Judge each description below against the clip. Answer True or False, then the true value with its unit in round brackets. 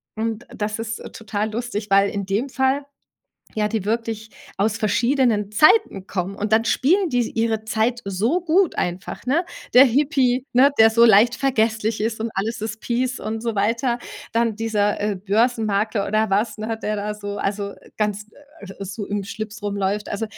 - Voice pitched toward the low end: False (220 Hz)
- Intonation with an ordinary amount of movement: False (2.3 semitones)